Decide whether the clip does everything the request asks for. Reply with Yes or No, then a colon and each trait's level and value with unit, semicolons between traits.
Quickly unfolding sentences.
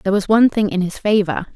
Yes: fast, 270 wpm